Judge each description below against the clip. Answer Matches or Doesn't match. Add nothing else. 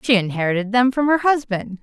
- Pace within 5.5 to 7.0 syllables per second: Matches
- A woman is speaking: Matches